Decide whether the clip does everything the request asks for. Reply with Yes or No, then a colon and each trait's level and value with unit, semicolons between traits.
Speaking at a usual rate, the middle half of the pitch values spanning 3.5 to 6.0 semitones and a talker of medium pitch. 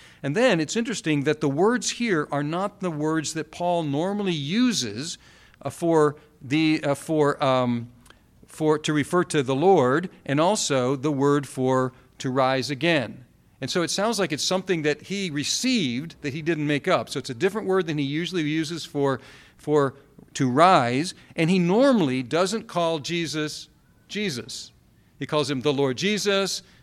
Yes: average, 170 wpm; average, 4.3 semitones; medium, 155 Hz